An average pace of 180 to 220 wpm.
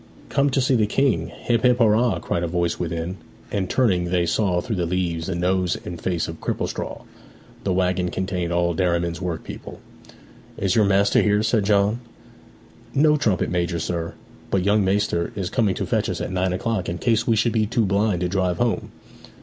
Yes: average, 190 wpm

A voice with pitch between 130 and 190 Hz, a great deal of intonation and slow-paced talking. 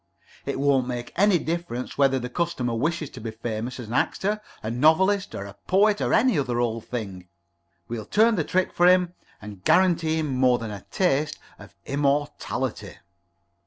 No: medium, 140 Hz; wide, 6.8 semitones; average, 175 wpm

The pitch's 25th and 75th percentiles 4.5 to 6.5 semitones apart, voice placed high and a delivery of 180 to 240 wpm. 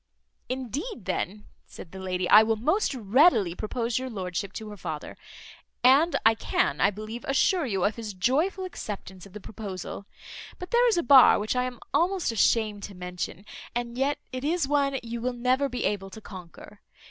Yes: average, 5.2 semitones; high, 230 Hz; average, 185 wpm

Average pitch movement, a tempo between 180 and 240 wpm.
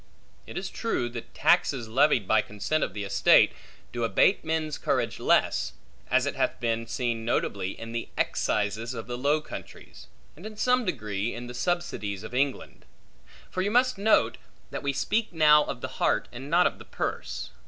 No: wide, 6.2 semitones; average, 185 wpm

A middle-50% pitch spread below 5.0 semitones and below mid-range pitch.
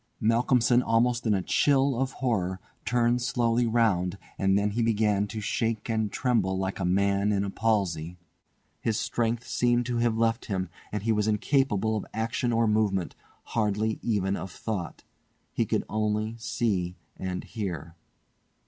Yes: average, 3.0 semitones; low, 110 Hz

